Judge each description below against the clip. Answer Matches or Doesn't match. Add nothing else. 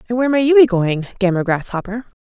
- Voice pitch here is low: Doesn't match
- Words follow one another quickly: Matches